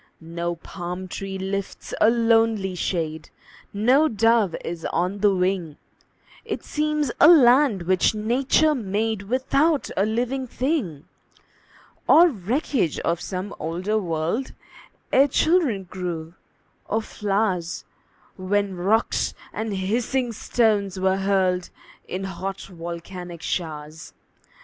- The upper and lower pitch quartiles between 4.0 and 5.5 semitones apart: Yes, average, 4.7 semitones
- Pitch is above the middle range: Yes, high, 195 Hz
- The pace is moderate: No, slow, 110 wpm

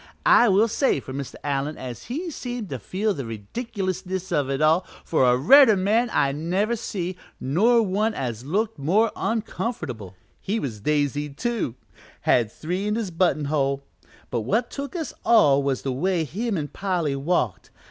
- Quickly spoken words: No, average, 170 wpm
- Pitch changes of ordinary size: No, wide, 7.9 semitones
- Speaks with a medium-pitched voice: Yes, medium, 175 Hz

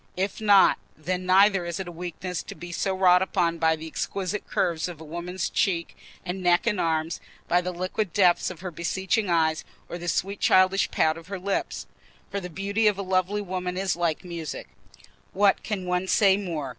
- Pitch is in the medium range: Yes, medium, 180 Hz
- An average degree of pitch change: No, narrow, 2.1 semitones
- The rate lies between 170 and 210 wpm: Yes, average, 200 wpm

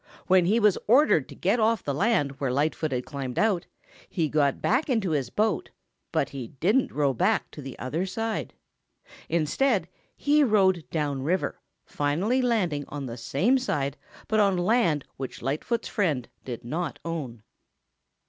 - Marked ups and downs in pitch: Yes, wide, 7.5 semitones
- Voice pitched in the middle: Yes, medium, 165 Hz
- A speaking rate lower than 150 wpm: No, average, 165 wpm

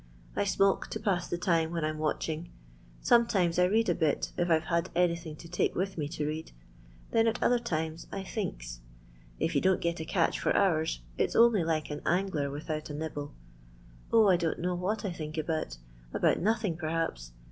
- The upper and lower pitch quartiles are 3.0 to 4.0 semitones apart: Yes, average, 3.4 semitones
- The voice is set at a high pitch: No, medium, 170 Hz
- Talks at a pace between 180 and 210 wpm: Yes, average, 200 wpm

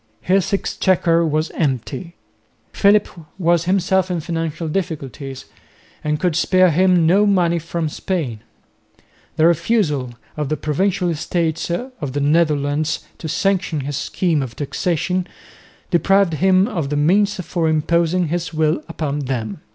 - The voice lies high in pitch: No, medium, 165 Hz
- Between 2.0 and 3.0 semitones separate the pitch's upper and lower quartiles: No, average, 3.4 semitones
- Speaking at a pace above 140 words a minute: No, slow, 135 wpm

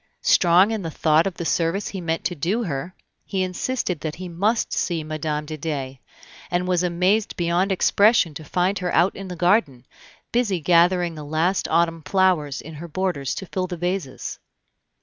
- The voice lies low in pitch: No, medium, 175 Hz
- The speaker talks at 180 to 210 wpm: Yes, average, 185 wpm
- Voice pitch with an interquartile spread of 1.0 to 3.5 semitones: Yes, average, 2.9 semitones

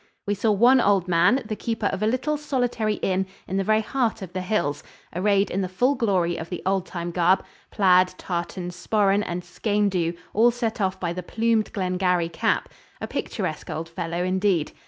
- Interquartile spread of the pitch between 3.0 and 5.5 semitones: Yes, average, 3.4 semitones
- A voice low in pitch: No, high, 195 Hz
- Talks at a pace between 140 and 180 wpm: No, average, 195 wpm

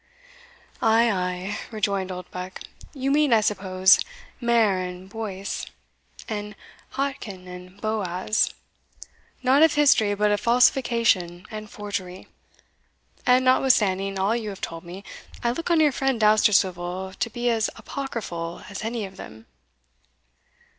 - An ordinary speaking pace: No, slow, 125 wpm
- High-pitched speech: Yes, high, 210 Hz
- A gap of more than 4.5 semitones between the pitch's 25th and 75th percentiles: No, average, 4.1 semitones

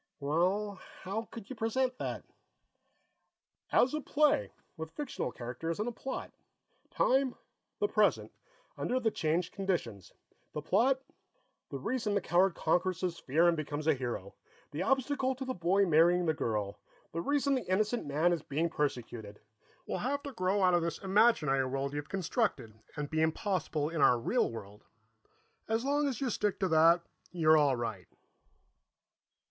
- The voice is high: No, medium, 175 Hz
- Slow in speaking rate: No, average, 160 wpm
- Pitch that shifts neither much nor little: No, wide, 7.3 semitones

